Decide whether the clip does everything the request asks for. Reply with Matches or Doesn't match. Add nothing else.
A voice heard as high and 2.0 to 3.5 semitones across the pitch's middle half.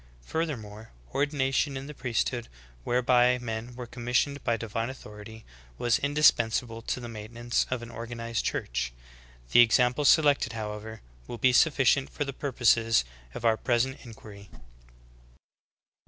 Doesn't match